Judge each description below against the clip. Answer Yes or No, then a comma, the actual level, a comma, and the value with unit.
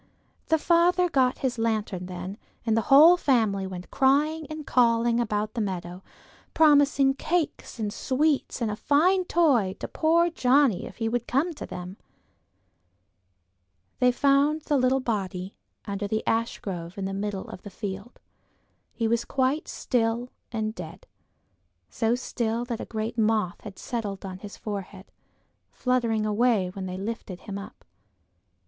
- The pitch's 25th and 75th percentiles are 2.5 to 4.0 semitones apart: No, average, 5.2 semitones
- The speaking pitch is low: No, high, 230 Hz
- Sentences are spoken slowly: No, average, 150 wpm